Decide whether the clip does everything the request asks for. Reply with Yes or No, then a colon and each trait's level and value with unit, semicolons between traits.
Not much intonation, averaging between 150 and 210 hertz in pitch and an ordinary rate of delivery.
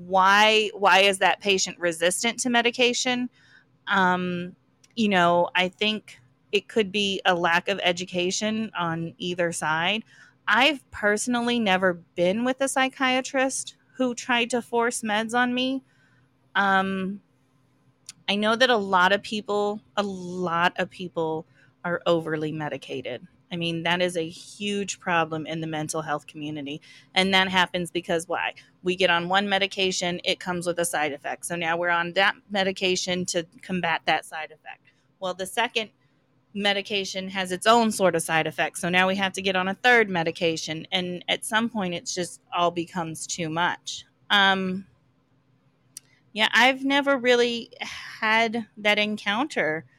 No: average, 4.1 semitones; medium, 185 Hz; average, 155 wpm